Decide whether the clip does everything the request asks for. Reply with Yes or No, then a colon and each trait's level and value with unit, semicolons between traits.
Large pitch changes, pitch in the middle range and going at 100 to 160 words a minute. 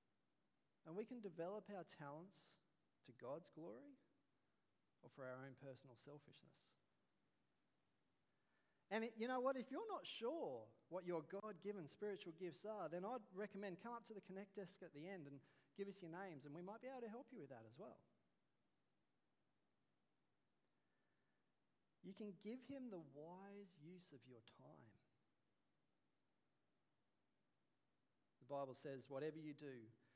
Yes: wide, 6.4 semitones; medium, 180 Hz; average, 150 wpm